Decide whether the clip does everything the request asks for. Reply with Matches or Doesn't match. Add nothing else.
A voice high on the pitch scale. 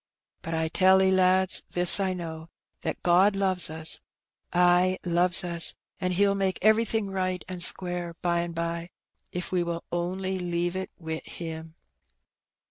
Doesn't match